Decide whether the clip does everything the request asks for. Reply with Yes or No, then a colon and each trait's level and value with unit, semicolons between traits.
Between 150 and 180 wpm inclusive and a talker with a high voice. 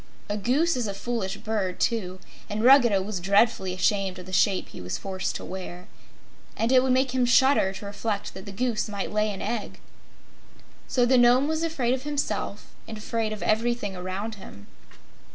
No: average, 190 wpm; high, 215 Hz